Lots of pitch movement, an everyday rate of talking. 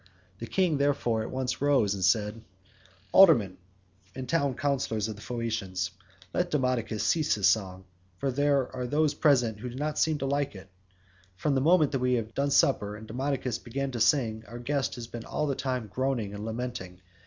No: average, 4.3 semitones; average, 190 wpm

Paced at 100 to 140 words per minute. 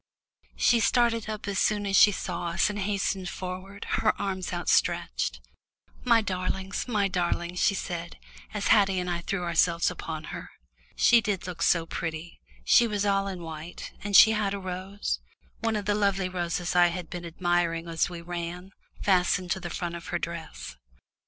No: average, 180 wpm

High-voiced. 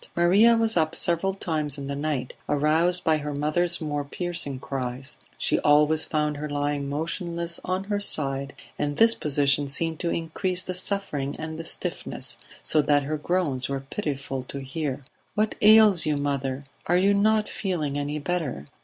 No: medium, 155 Hz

